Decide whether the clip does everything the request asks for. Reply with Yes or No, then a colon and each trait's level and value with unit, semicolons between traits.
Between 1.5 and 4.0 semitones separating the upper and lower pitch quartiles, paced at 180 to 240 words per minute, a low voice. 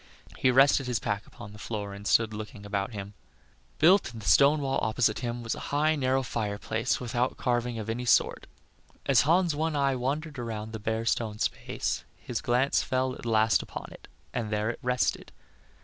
Yes: average, 3.6 semitones; average, 195 wpm; low, 120 Hz